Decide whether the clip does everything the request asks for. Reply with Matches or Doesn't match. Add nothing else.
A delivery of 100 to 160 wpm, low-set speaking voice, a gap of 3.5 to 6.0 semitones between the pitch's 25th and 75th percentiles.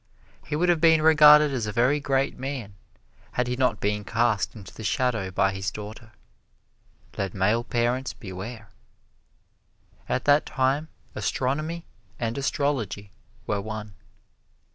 Matches